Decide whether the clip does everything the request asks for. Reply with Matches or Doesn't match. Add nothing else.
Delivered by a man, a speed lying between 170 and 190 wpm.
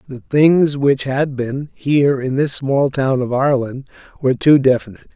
Matches